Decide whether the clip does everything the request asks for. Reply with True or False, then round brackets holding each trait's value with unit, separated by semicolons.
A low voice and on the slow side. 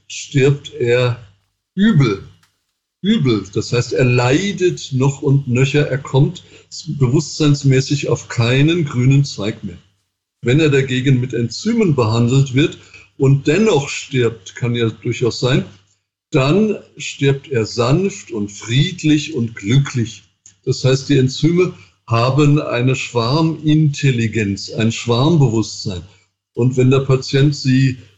True (130 Hz; 115 wpm)